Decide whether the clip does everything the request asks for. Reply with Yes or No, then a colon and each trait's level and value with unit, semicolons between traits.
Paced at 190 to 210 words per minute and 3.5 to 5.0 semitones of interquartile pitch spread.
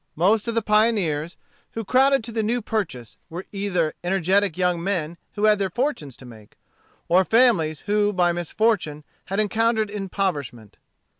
No: average, 155 wpm; average, 4.7 semitones